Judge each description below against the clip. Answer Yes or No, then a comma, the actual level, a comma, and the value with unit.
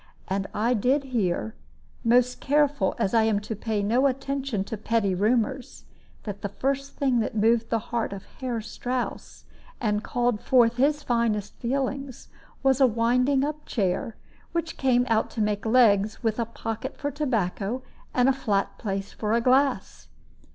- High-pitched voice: Yes, high, 235 Hz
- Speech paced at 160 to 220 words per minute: Yes, average, 165 wpm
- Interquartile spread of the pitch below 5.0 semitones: Yes, average, 3.8 semitones